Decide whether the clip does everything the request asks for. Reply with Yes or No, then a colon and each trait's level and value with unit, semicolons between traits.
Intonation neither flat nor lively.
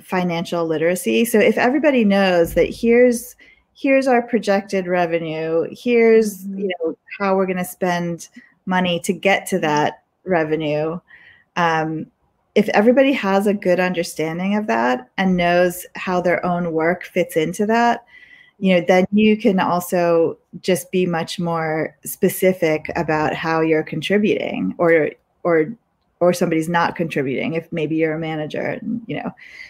Yes: average, 3.8 semitones